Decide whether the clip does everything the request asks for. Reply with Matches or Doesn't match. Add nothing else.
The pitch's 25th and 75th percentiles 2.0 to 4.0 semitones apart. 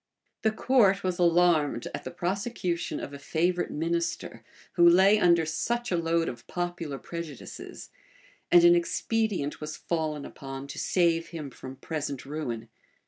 Matches